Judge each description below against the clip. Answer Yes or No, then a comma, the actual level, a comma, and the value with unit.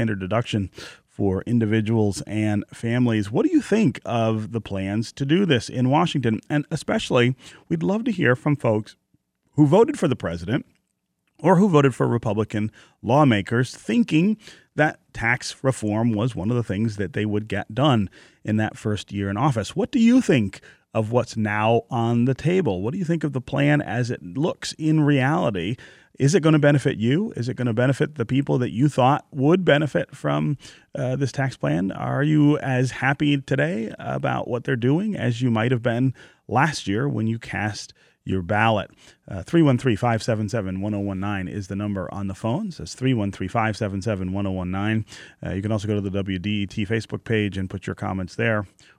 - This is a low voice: Yes, low, 120 Hz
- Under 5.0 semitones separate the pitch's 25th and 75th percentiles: No, wide, 5.4 semitones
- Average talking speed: Yes, average, 180 wpm